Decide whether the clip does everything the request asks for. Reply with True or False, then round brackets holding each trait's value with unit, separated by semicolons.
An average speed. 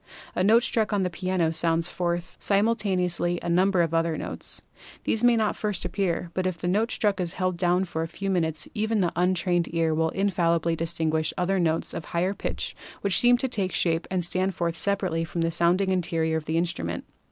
False (210 wpm)